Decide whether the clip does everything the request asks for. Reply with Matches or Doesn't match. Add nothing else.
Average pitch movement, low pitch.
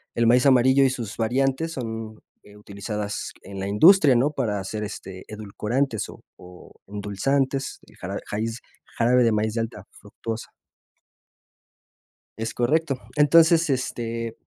Matches